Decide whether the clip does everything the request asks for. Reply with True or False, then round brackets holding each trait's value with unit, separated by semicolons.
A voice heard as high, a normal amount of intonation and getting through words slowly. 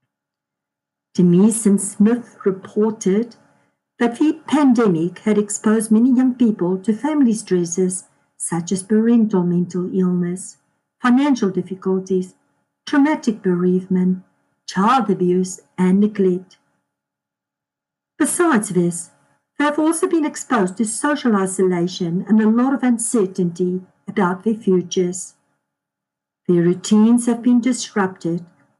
True (195 Hz; 4.4 semitones; 105 wpm)